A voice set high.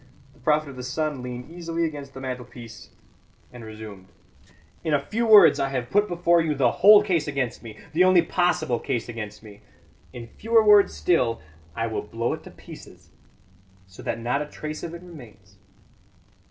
No: medium, 140 Hz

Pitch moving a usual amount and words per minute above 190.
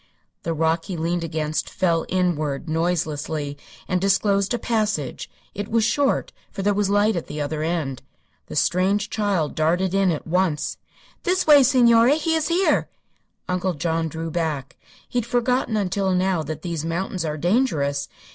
No: average, 4.5 semitones; average, 165 wpm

